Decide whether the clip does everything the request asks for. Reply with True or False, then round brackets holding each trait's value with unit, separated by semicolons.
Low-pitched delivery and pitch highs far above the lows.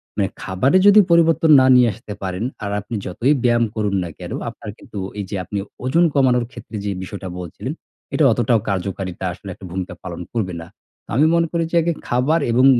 True (115 Hz; 5.7 semitones)